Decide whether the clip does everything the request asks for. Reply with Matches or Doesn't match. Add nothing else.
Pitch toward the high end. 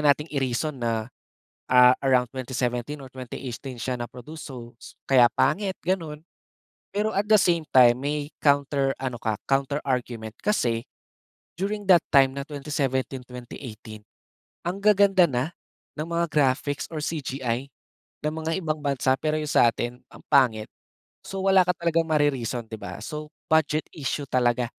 Doesn't match